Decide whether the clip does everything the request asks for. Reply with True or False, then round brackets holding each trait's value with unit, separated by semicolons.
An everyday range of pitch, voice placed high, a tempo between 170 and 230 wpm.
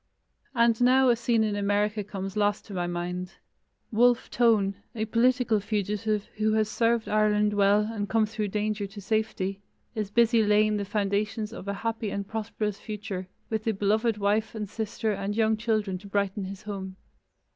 False (1.7 semitones; 210 Hz; 175 wpm)